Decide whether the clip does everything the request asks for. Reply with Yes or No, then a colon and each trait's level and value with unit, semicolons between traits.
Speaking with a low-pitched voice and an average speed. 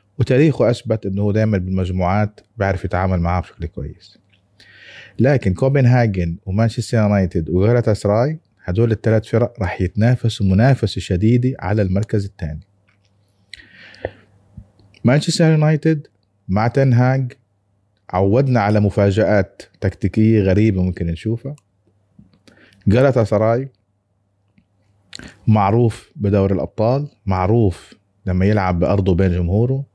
Yes: low, 105 Hz; average, 95 wpm